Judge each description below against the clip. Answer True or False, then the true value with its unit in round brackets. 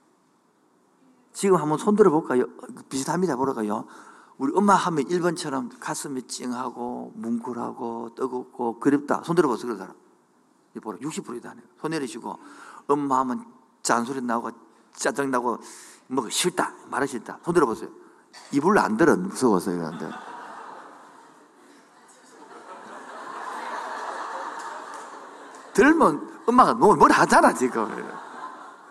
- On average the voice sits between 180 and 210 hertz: False (130 Hz)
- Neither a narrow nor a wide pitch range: True (4.0 semitones)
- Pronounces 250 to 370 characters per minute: False (235 characters per minute)